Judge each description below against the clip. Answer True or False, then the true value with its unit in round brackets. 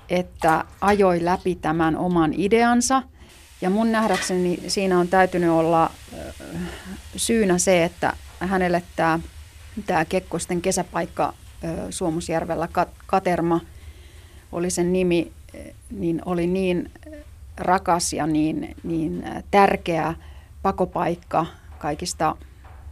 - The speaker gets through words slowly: True (90 wpm)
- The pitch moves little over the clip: True (2.3 semitones)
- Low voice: False (175 Hz)